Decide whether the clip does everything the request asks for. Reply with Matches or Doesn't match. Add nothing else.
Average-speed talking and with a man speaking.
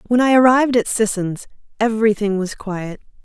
Doesn't match